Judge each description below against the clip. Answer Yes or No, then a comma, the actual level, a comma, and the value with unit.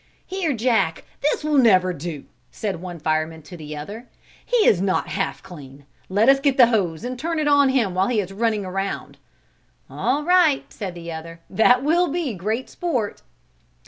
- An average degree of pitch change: No, wide, 7.6 semitones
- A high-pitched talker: Yes, high, 210 Hz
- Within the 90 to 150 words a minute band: No, average, 180 wpm